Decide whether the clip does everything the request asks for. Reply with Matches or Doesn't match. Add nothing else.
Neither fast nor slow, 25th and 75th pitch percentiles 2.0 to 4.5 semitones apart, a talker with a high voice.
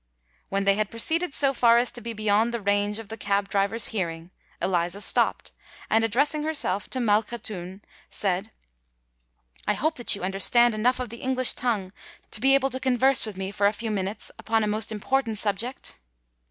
Matches